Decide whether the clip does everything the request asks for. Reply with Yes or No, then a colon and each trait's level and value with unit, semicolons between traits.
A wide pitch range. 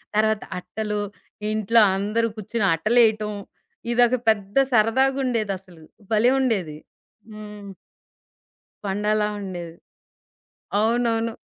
No: narrow, 2.4 semitones